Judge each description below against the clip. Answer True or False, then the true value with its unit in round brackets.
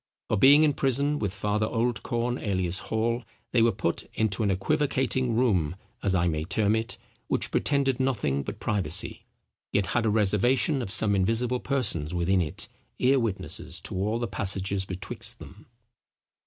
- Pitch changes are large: False (4.4 semitones)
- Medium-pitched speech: False (110 Hz)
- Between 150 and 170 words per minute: True (160 wpm)